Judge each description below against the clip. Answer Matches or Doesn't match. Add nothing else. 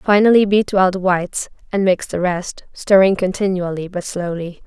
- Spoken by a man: Doesn't match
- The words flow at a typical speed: Matches